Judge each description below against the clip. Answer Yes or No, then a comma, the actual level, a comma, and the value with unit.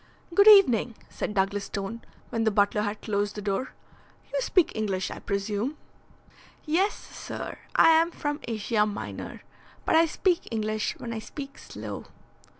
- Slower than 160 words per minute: Yes, average, 150 wpm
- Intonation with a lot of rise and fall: Yes, wide, 6.9 semitones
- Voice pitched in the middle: No, high, 220 Hz